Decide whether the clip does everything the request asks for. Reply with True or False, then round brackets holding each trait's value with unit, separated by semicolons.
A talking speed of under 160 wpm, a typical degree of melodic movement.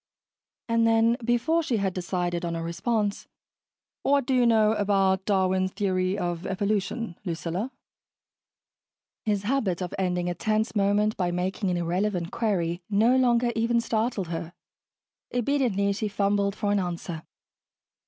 True (140 wpm; 3.9 semitones)